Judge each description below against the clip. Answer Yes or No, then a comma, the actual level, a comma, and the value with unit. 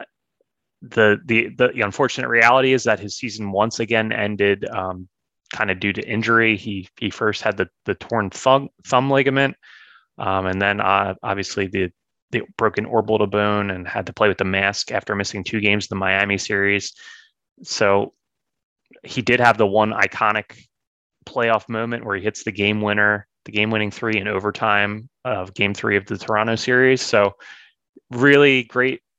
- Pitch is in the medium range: No, low, 105 Hz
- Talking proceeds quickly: No, average, 175 wpm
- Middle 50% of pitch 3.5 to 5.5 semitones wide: No, narrow, 2.5 semitones